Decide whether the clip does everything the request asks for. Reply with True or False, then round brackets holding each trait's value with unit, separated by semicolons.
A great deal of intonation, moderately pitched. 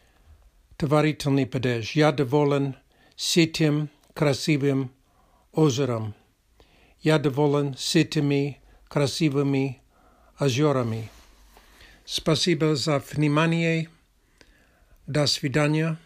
False (2.4 semitones; 145 Hz)